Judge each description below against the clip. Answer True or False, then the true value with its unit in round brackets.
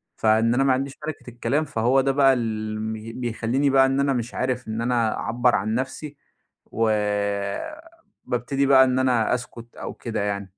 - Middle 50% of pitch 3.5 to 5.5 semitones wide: False (3.0 semitones)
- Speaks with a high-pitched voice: False (125 Hz)